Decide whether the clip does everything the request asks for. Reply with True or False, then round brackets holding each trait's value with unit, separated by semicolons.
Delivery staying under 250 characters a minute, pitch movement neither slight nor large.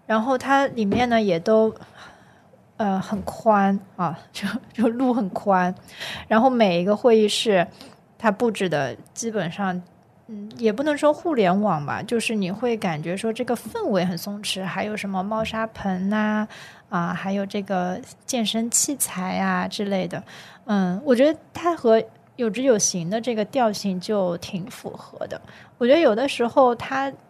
True (230 characters per minute; 3.7 semitones)